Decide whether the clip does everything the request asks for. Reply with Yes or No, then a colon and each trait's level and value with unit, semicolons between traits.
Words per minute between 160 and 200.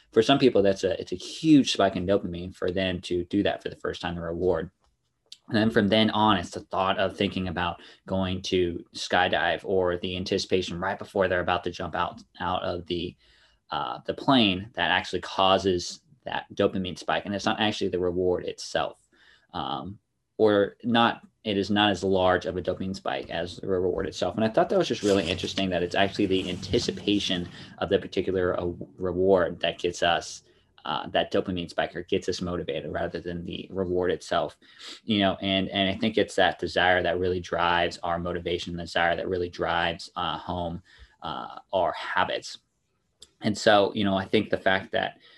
Yes: average, 195 wpm